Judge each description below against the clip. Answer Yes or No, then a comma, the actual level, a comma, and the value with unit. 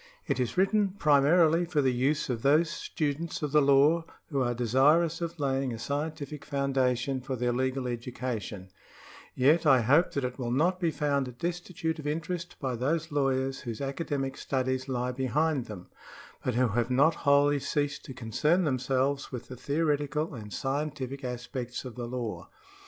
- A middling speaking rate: Yes, average, 170 wpm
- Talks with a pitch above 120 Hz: Yes, low, 135 Hz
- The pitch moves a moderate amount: Yes, average, 3.3 semitones